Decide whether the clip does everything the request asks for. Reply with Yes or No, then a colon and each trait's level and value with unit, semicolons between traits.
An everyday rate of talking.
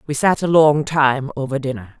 No: fast, 210 wpm